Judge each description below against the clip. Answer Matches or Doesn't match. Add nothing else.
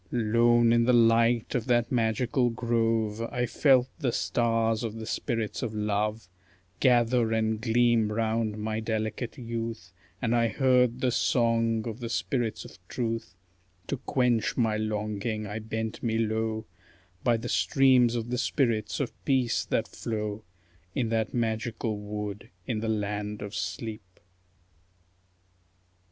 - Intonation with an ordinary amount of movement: Doesn't match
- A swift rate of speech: Doesn't match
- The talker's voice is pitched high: Doesn't match